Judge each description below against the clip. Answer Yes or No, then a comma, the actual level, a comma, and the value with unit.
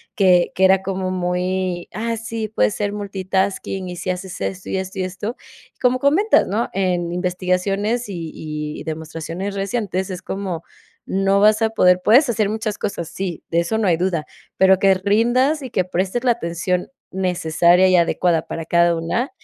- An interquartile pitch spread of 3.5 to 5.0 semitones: No, average, 2.8 semitones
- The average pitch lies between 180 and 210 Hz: Yes, high, 190 Hz